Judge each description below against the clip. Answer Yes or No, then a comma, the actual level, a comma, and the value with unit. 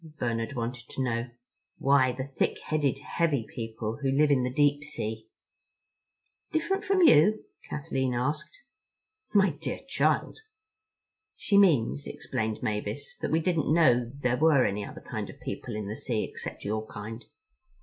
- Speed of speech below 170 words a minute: Yes, average, 150 wpm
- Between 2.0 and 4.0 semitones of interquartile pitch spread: No, average, 5.0 semitones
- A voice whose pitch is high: No, low, 130 Hz